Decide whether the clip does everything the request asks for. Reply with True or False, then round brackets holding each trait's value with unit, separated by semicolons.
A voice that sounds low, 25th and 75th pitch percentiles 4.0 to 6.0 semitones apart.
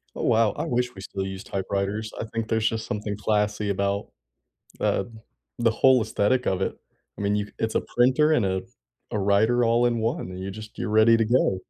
False (110 Hz; 2.4 semitones)